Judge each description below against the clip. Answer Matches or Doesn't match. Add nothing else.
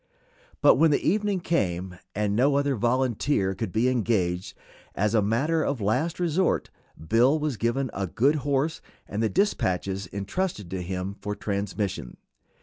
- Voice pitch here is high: Doesn't match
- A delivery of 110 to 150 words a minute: Matches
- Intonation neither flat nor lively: Doesn't match